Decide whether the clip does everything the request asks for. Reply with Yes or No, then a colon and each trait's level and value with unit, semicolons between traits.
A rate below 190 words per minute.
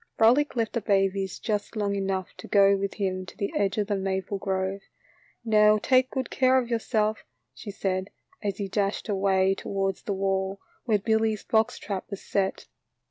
Yes: average, 180 wpm